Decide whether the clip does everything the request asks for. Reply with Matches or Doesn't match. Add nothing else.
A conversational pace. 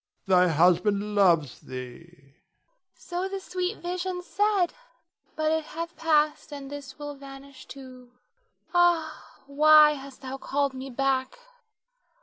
Doesn't match